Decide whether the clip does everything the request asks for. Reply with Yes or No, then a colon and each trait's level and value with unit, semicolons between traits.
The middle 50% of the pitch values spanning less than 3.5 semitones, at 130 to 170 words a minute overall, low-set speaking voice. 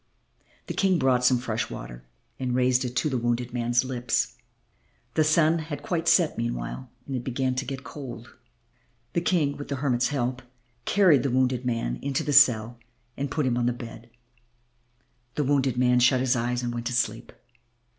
No: average, 2.7 semitones; average, 185 wpm; low, 125 Hz